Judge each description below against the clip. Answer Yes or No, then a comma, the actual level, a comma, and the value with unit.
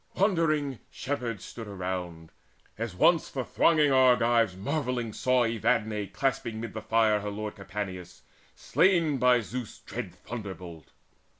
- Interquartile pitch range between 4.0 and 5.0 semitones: Yes, average, 4.4 semitones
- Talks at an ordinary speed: No, slow, 125 wpm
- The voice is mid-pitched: No, low, 115 Hz